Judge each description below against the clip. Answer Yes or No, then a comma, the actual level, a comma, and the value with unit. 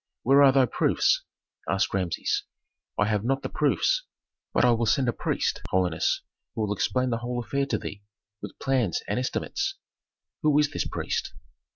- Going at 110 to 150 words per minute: No, average, 175 wpm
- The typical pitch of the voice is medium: No, low, 120 Hz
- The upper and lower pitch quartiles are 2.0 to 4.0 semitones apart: No, average, 4.9 semitones